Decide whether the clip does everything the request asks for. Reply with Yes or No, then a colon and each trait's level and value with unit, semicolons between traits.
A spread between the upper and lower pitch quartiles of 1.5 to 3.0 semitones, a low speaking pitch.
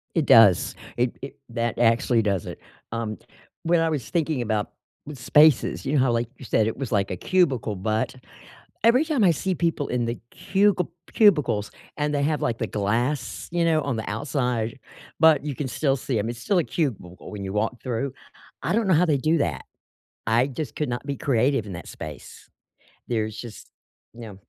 No: wide, 5.5 semitones; low, 125 Hz